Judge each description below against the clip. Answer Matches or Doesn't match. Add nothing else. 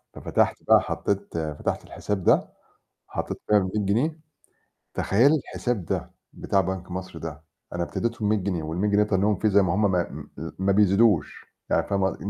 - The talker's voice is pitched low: Matches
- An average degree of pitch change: Doesn't match